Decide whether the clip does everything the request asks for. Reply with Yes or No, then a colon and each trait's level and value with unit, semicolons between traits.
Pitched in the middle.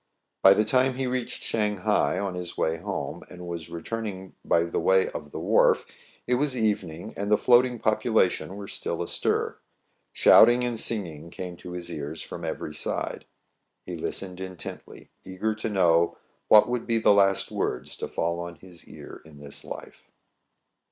No: very low, 95 Hz